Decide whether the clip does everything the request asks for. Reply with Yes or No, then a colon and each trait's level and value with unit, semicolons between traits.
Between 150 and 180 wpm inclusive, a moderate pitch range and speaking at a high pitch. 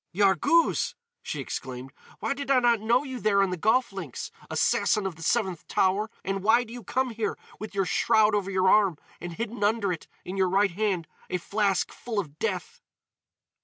No: average, 195 wpm; average, 3.5 semitones; high, 205 Hz